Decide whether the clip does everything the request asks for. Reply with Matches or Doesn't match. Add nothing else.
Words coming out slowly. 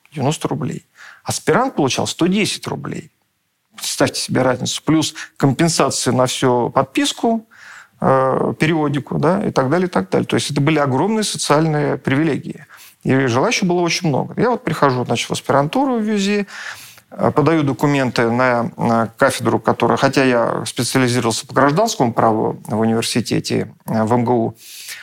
Doesn't match